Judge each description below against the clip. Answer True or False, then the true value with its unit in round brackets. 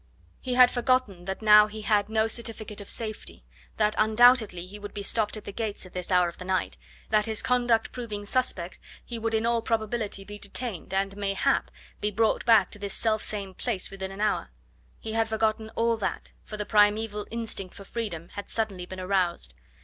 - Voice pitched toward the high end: True (210 Hz)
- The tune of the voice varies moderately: False (2.3 semitones)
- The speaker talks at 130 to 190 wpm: False (200 wpm)